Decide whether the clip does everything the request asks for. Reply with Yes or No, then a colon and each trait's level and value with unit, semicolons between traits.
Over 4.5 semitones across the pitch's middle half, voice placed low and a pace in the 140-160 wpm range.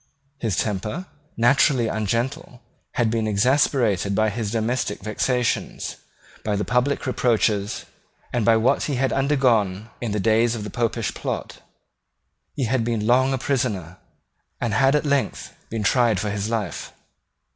No: average, 3.2 semitones; low, 115 Hz; average, 145 wpm